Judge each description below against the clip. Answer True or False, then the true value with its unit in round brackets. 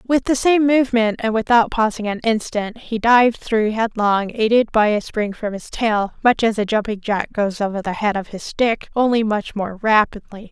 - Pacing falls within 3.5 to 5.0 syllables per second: True (4.8 syllables/s)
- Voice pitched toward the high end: True (220 Hz)